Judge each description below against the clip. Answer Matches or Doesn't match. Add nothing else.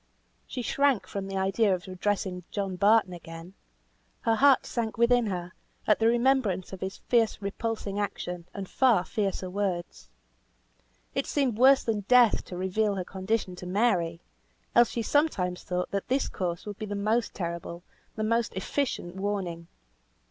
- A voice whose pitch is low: Doesn't match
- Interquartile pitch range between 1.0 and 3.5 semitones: Doesn't match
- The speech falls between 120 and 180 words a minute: Matches